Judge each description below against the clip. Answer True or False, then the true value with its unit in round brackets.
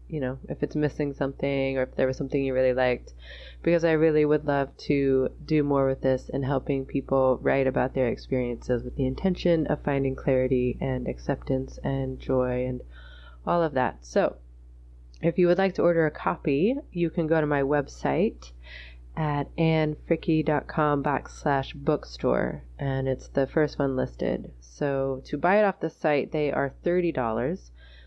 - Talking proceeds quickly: False (170 wpm)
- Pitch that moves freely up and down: False (3.0 semitones)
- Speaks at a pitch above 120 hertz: True (135 Hz)